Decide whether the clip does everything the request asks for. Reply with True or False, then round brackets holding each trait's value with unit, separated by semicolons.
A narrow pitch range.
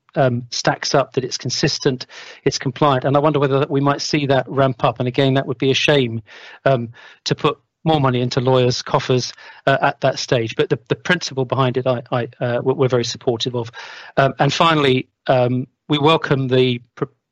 True (2.3 semitones)